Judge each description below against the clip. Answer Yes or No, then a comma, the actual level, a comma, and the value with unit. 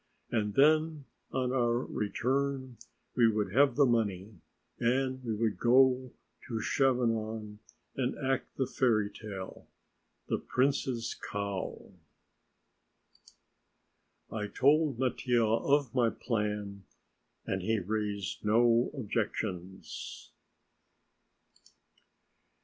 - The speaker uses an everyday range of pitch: Yes, average, 3.7 semitones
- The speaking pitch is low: Yes, low, 120 Hz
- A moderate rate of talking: No, slow, 95 wpm